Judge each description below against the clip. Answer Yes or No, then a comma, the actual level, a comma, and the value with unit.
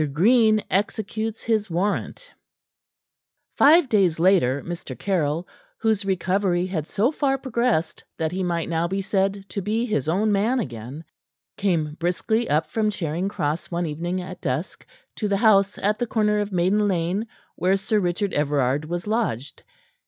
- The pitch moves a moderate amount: Yes, average, 4.2 semitones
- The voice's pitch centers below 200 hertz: Yes, high, 190 Hz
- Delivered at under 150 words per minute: No, average, 155 wpm